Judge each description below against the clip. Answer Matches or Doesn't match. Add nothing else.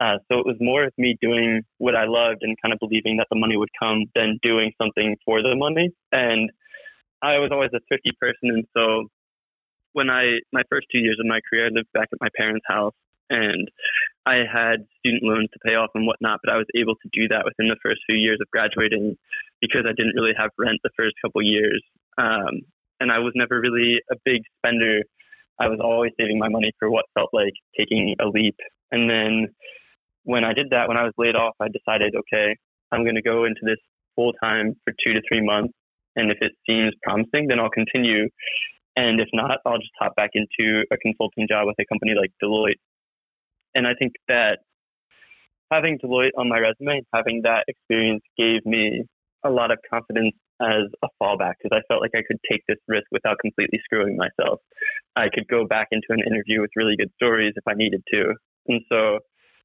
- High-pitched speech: Doesn't match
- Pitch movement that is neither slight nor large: Doesn't match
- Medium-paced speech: Doesn't match